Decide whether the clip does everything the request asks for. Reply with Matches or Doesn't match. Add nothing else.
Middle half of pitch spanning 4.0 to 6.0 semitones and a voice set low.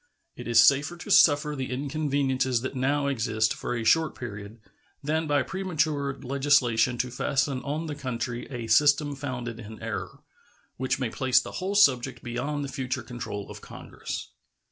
Doesn't match